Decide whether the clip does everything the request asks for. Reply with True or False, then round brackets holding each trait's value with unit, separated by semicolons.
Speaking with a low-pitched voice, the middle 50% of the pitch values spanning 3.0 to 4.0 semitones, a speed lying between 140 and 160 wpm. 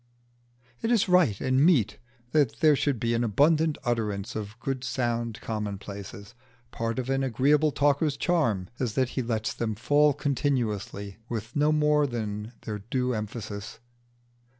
False (120 Hz; 5.1 semitones; 150 wpm)